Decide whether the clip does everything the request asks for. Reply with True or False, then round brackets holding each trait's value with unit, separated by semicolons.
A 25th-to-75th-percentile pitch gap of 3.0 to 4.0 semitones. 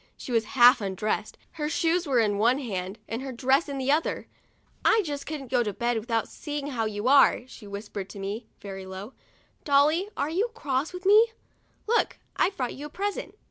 False (5.6 semitones)